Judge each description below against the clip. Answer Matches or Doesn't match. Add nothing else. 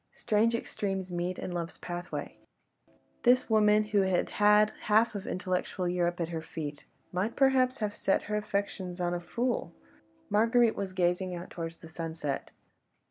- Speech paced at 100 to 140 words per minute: Doesn't match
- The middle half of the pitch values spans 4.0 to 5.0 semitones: Doesn't match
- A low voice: Doesn't match